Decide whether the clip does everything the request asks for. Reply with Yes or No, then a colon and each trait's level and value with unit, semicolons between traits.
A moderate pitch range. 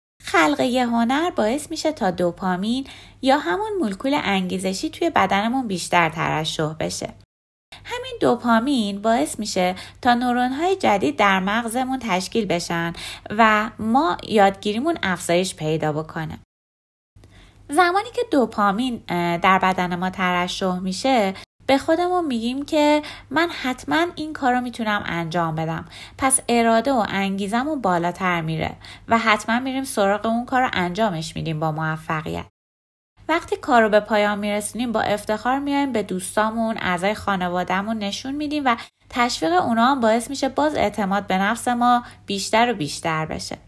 No: wide, 6.2 semitones